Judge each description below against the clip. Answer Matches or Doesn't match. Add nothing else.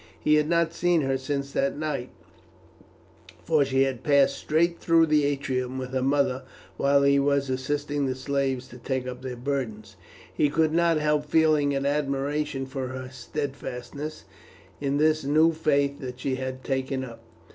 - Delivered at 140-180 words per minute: Matches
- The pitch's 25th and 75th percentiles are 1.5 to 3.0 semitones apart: Matches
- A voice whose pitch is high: Doesn't match